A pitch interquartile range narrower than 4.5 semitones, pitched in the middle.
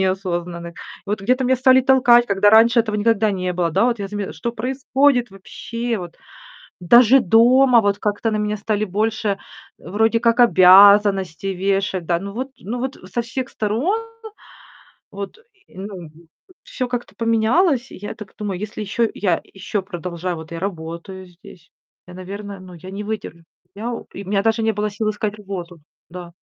No: average, 3.7 semitones; high, 205 Hz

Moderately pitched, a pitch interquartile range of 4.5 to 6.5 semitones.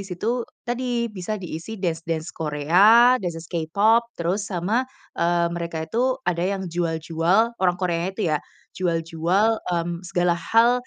Yes: medium, 180 Hz; average, 4.8 semitones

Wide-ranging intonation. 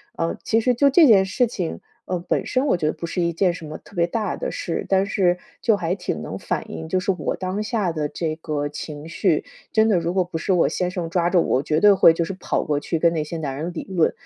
No: average, 3.2 semitones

